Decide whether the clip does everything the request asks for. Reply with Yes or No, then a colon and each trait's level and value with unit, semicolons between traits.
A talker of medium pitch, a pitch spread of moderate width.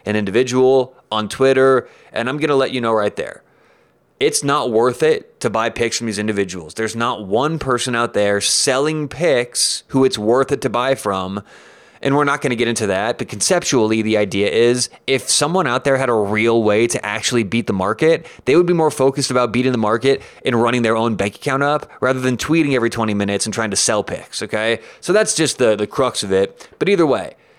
No: low, 120 Hz; average, 3.9 semitones